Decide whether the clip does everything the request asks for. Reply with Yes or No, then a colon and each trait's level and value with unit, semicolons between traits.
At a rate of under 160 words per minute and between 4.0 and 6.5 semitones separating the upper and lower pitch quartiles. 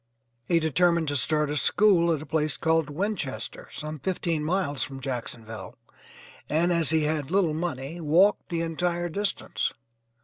No: average, 150 wpm; average, 2.9 semitones